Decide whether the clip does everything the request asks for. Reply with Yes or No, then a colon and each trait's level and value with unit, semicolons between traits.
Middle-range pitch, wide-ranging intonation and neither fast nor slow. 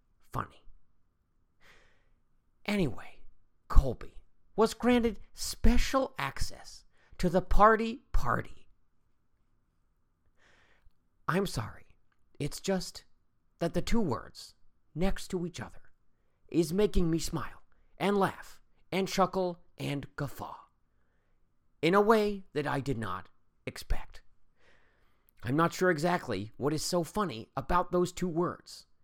No: medium, 175 Hz; wide, 7.1 semitones; slow, 110 wpm